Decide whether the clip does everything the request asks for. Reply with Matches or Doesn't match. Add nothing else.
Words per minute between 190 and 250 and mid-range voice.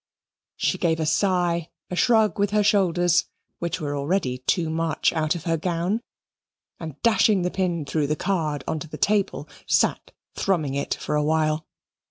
Doesn't match